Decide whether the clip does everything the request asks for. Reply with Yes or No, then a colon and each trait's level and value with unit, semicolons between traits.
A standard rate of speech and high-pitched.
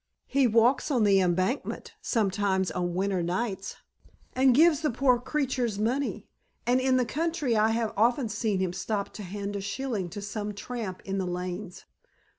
Yes: average, 170 wpm; high, 215 Hz